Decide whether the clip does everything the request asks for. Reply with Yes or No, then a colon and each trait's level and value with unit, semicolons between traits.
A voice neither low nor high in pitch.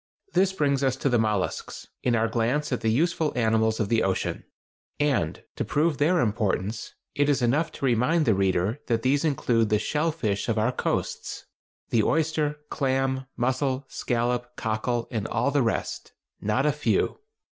No: low, 125 Hz